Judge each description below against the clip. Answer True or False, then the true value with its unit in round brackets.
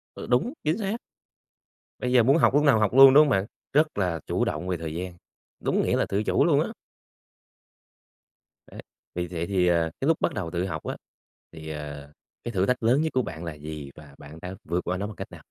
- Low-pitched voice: True (95 Hz)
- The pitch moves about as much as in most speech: False (7.5 semitones)